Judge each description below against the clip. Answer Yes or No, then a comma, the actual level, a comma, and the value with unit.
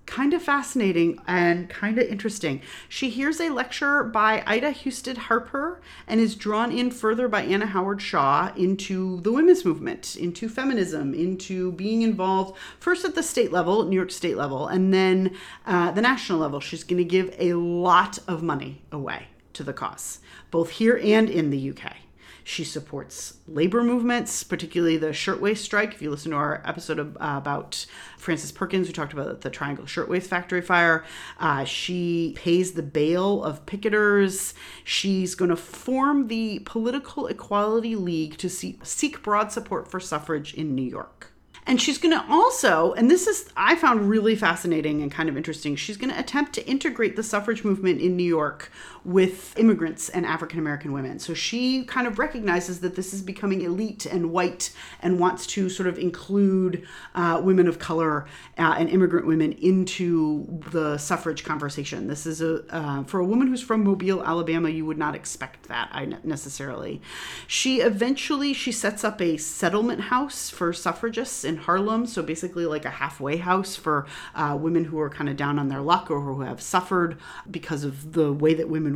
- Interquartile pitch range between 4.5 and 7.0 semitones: Yes, average, 5.3 semitones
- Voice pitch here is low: No, medium, 180 Hz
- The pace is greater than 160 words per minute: Yes, average, 175 wpm